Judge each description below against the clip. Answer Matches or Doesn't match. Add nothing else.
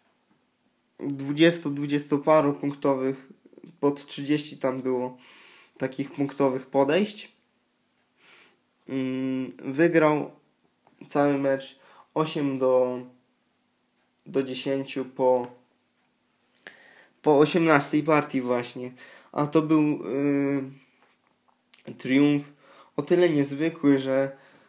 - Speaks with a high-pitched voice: Doesn't match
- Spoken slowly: Matches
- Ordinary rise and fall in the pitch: Doesn't match